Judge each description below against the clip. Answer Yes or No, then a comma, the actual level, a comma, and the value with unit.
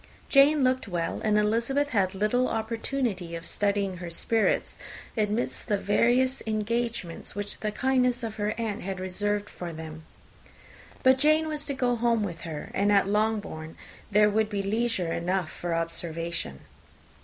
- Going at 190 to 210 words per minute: No, average, 155 wpm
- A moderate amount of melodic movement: Yes, average, 4.6 semitones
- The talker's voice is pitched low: No, high, 210 Hz